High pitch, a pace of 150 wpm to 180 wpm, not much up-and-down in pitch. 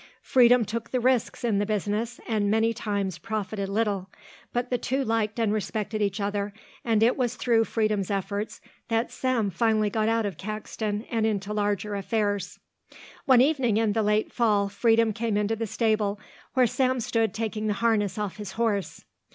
Yes: high, 215 Hz; average, 175 wpm; narrow, 2.0 semitones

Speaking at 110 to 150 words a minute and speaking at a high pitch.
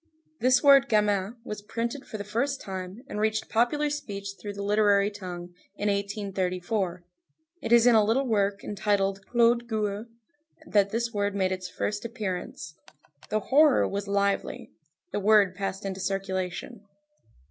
Yes: average, 145 wpm; high, 205 Hz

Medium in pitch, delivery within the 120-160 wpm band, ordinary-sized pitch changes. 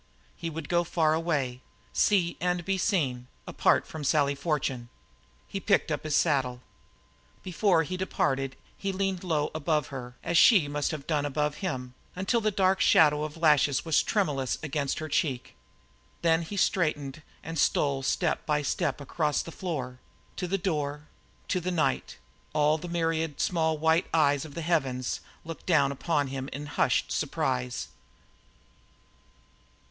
Yes: medium, 155 Hz; average, 155 wpm; average, 3.4 semitones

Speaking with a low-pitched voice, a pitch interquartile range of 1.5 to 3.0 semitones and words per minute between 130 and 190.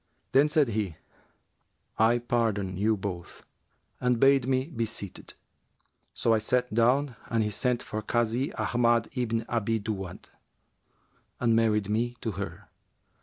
Yes: low, 115 Hz; narrow, 2.4 semitones; average, 140 wpm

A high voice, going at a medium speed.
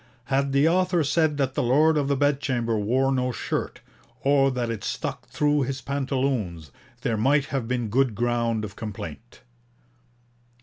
No: low, 135 Hz; average, 160 wpm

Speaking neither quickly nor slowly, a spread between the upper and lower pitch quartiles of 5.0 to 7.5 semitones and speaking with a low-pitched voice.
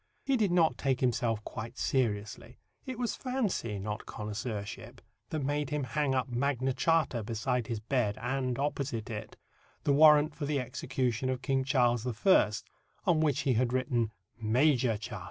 No: average, 160 wpm; average, 4.1 semitones; low, 130 Hz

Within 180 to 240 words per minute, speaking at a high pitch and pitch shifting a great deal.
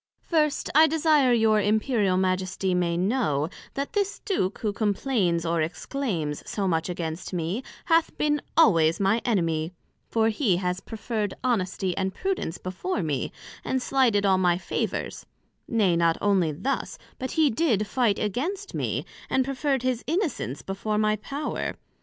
No: average, 150 wpm; high, 210 Hz; wide, 6.6 semitones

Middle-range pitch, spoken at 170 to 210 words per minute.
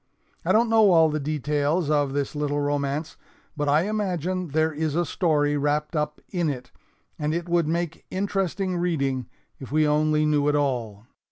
Yes: medium, 150 Hz; average, 175 wpm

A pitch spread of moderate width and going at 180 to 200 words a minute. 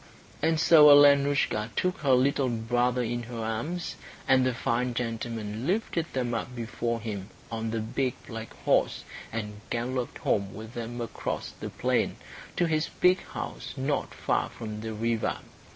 No: average, 3.6 semitones; average, 155 wpm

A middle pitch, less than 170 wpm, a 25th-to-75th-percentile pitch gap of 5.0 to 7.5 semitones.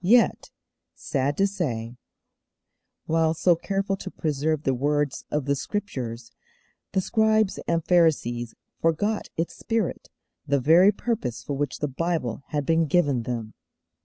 Yes: medium, 155 Hz; slow, 135 wpm; wide, 5.5 semitones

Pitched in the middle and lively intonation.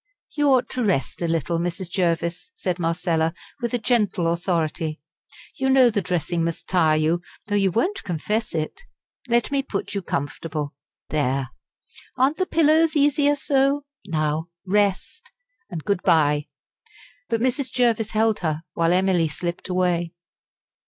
Yes: medium, 180 Hz; wide, 6.4 semitones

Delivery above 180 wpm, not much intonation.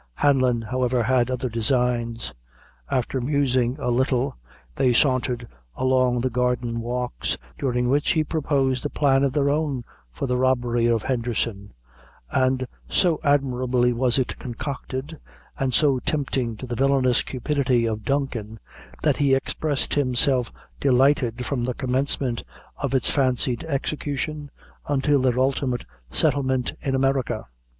No: slow, 135 wpm; narrow, 2.1 semitones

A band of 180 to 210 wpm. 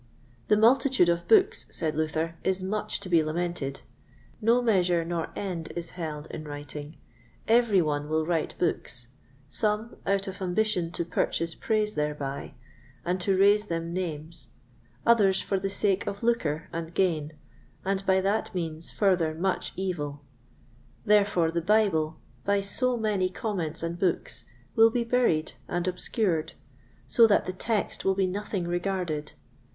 No: average, 150 wpm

